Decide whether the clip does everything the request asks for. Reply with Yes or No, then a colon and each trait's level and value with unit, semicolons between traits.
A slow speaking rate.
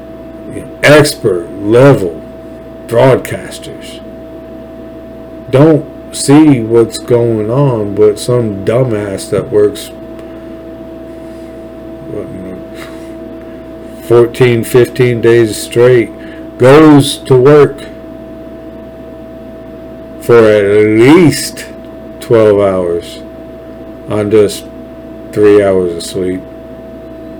Yes: slow, 70 wpm